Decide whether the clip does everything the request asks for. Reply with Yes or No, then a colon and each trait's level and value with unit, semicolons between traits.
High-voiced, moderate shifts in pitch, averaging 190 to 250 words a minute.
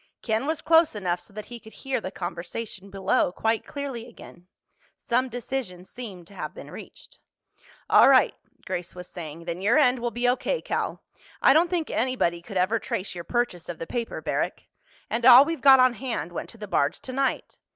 No: high, 225 Hz; wide, 6.0 semitones; average, 195 wpm